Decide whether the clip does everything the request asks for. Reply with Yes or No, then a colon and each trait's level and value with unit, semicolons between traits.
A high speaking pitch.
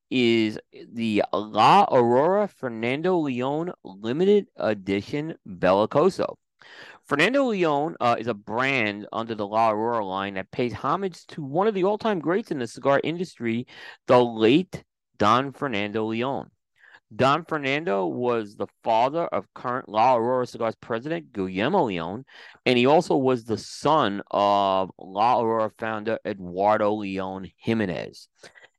No: low, 120 Hz